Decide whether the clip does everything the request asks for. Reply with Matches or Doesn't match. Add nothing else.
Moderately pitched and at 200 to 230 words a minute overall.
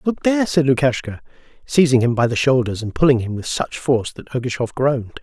Doesn't match